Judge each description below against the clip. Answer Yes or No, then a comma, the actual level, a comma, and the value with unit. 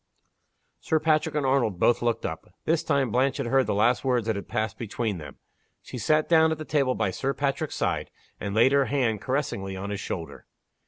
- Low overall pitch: Yes, low, 130 Hz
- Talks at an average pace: No, fast, 210 wpm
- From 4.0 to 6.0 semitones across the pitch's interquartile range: Yes, average, 4.7 semitones